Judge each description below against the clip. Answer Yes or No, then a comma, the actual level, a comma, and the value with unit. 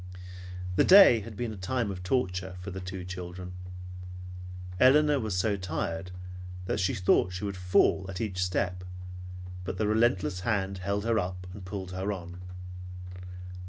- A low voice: Yes, very low, 95 Hz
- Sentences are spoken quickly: No, average, 160 wpm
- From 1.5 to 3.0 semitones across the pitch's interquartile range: Yes, average, 2.7 semitones